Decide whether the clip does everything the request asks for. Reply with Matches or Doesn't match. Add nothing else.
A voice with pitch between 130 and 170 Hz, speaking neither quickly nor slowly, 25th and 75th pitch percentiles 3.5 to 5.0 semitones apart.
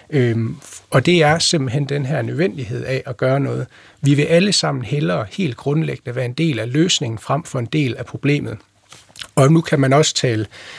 Matches